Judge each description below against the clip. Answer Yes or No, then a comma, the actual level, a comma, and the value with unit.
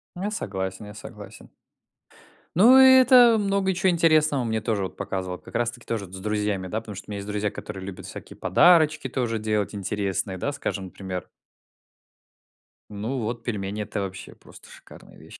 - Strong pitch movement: Yes, wide, 7.5 semitones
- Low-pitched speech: Yes, low, 105 Hz